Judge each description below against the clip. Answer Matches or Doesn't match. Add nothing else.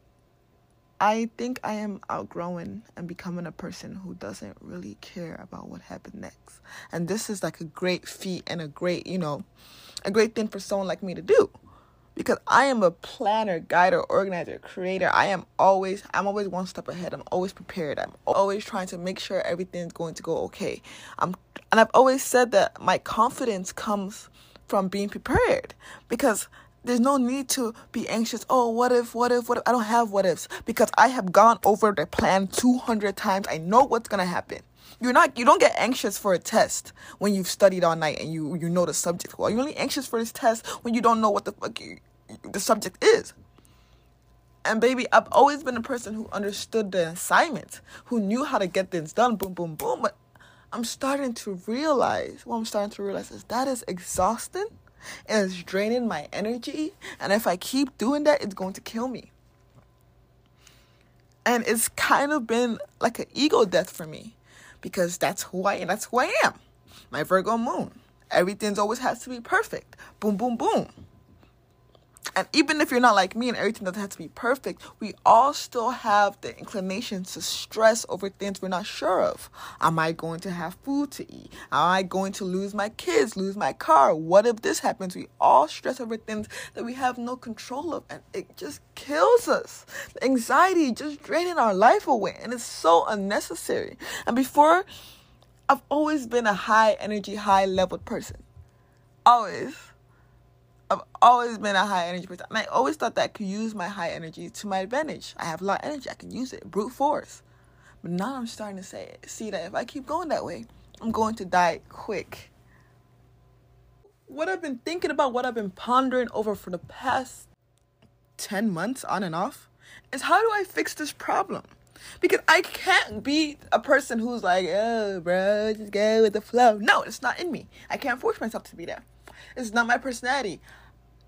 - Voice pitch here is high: Matches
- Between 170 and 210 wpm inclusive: Matches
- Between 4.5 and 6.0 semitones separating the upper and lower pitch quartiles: Matches